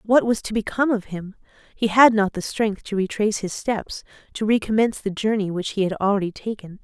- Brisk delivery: Yes, fast, 210 wpm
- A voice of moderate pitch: No, high, 210 Hz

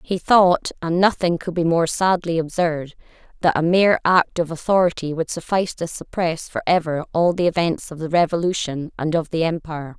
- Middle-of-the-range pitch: Yes, medium, 170 Hz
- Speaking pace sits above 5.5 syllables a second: No, 5.3 syllables/s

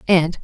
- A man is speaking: No, female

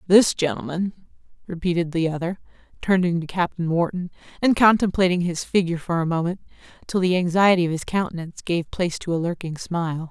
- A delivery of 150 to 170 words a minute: Yes, average, 165 wpm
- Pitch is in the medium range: Yes, medium, 175 Hz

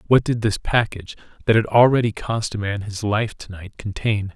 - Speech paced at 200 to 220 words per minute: Yes, fast, 205 wpm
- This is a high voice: No, low, 110 Hz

